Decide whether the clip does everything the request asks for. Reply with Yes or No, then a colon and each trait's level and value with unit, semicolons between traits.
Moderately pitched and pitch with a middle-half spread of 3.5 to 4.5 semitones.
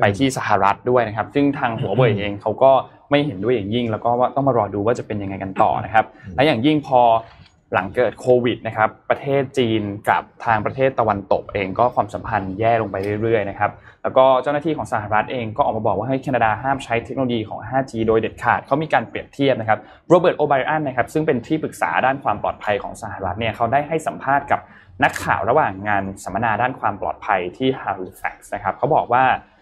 No: low, 115 Hz; average, 3.8 semitones